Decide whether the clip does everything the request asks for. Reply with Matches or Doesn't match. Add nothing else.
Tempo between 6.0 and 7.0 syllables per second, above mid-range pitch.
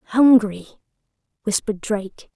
Doesn't match